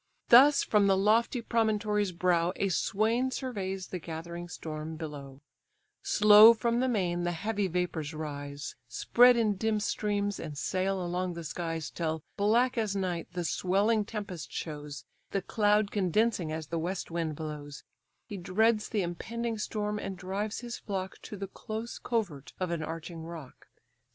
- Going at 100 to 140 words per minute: No, average, 155 wpm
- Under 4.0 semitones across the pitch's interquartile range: No, average, 4.4 semitones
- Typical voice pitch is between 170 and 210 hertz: Yes, high, 190 Hz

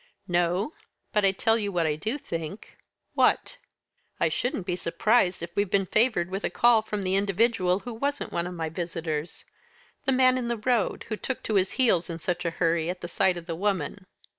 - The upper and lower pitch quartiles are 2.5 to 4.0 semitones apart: No, average, 4.5 semitones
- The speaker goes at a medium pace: No, fast, 210 wpm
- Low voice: No, high, 190 Hz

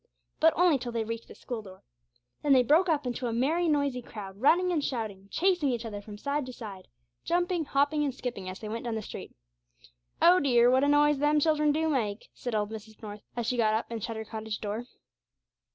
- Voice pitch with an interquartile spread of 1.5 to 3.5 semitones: No, average, 5.2 semitones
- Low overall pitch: No, high, 245 Hz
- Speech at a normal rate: No, fast, 225 wpm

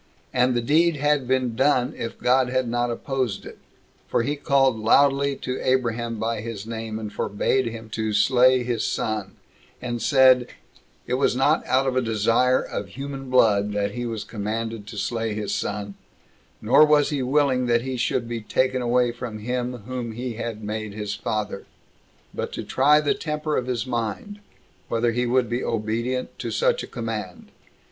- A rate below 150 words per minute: No, average, 180 wpm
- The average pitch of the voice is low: Yes, low, 120 Hz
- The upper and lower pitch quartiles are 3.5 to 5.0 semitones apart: No, average, 2.7 semitones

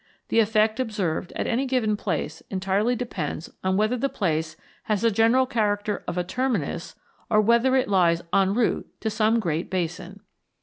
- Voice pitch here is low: No, high, 210 Hz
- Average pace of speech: Yes, average, 170 wpm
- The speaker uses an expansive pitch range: No, average, 4.1 semitones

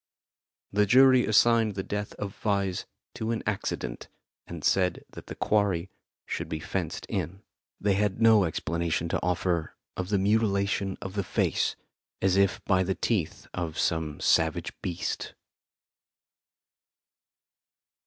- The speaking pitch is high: No, very low, 95 Hz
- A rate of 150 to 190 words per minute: No, slow, 135 wpm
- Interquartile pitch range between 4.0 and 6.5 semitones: No, average, 3.0 semitones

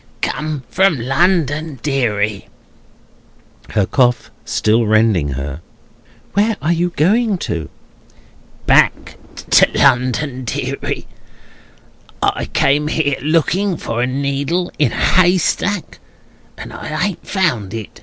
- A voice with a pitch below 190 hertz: Yes, medium, 140 Hz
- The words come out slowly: Yes, slow, 110 wpm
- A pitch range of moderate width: No, wide, 7.2 semitones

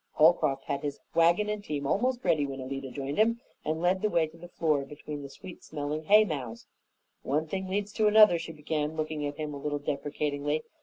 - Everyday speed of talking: No, fast, 210 wpm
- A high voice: No, medium, 155 Hz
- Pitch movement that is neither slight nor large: Yes, average, 3.7 semitones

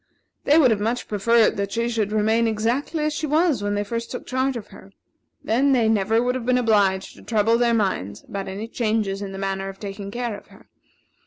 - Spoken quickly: Yes, fast, 225 wpm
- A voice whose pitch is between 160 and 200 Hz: No, high, 225 Hz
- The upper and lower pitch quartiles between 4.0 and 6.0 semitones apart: No, average, 3.3 semitones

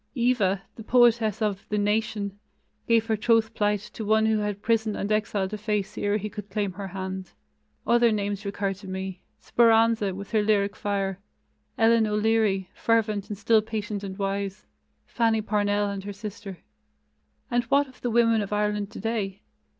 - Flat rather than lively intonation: Yes, narrow, 1.9 semitones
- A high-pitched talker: Yes, high, 210 Hz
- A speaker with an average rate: Yes, average, 170 wpm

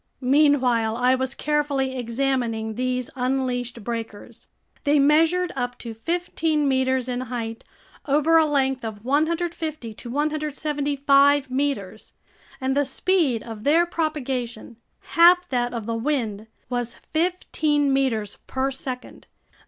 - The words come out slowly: Yes, slow, 120 wpm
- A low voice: No, very high, 265 Hz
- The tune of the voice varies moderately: Yes, average, 3.6 semitones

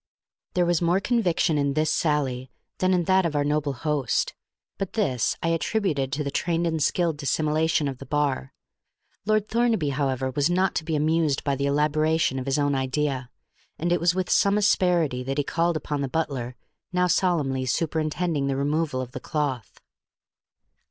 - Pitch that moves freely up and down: No, average, 3.8 semitones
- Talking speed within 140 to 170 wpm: No, average, 180 wpm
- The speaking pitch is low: No, medium, 150 Hz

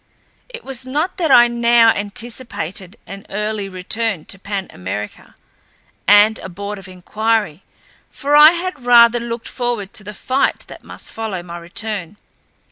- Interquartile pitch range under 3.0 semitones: No, average, 3.6 semitones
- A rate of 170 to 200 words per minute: No, average, 150 wpm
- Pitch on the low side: No, high, 220 Hz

